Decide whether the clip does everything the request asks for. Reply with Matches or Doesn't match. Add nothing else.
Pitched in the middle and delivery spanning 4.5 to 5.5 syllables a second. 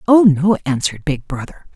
Matches